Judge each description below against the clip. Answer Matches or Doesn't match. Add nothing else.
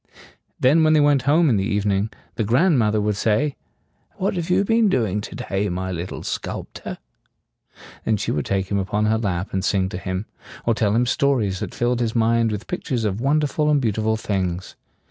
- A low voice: Matches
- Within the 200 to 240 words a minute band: Matches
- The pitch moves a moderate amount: Doesn't match